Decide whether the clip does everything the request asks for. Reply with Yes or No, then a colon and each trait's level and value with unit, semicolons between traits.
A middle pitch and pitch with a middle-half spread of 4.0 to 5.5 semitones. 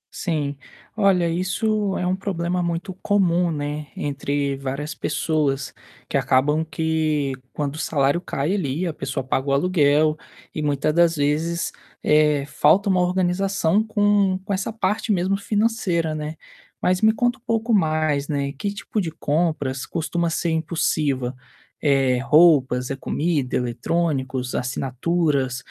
Yes: medium, 160 Hz; average, 4.4 semitones